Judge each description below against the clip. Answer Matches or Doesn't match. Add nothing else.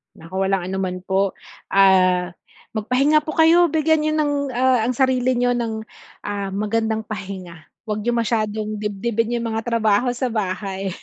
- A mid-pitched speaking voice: Doesn't match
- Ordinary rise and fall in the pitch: Matches